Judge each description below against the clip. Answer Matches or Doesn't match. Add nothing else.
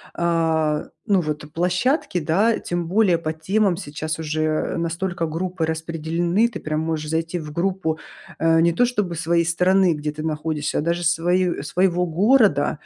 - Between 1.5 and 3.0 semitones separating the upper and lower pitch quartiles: Matches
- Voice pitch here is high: Doesn't match